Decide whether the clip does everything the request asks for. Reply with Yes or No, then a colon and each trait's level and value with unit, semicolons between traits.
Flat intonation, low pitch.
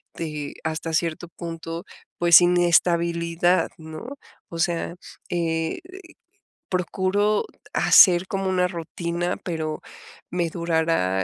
No: narrow, 1.5 semitones; medium, 170 Hz